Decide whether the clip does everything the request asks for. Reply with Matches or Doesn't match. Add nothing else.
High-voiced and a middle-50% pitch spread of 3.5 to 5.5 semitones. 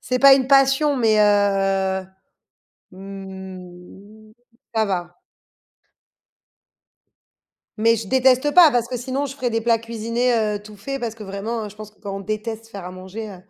Matches